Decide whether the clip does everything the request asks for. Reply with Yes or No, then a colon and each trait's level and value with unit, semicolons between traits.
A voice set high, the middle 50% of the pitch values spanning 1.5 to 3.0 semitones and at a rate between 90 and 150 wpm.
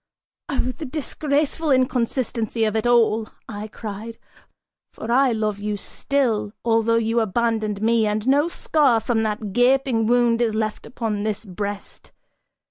Yes: high, 225 Hz; narrow, 2.6 semitones; average, 140 wpm